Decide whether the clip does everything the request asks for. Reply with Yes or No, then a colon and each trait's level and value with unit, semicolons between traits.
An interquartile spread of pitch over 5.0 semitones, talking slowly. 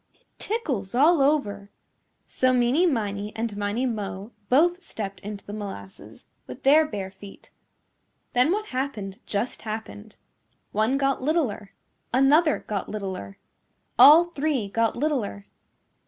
Yes: wide, 5.6 semitones; slow, 125 wpm